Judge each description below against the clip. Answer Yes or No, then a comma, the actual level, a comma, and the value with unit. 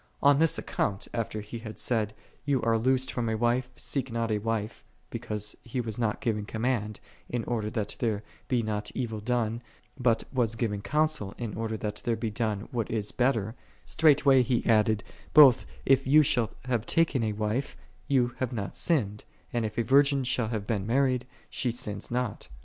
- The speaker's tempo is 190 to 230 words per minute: Yes, average, 195 wpm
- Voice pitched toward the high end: No, low, 115 Hz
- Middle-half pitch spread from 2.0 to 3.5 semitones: Yes, average, 2.9 semitones